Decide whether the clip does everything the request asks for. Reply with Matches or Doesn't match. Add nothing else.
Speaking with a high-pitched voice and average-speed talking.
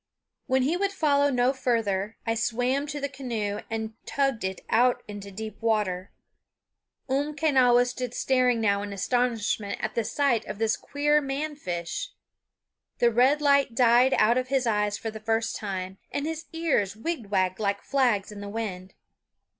Matches